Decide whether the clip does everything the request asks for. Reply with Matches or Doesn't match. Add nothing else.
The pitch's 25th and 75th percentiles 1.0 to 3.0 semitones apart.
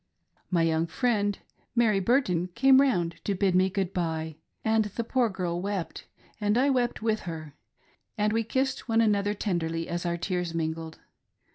Doesn't match